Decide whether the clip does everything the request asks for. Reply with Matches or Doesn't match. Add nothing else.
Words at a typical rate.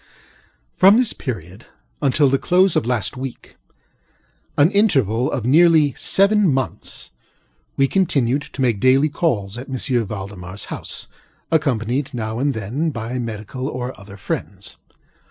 Doesn't match